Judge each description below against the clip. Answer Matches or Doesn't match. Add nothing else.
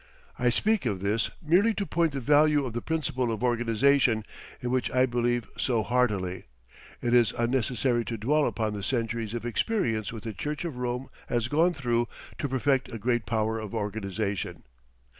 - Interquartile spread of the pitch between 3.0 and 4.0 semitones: Matches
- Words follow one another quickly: Doesn't match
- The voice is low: Matches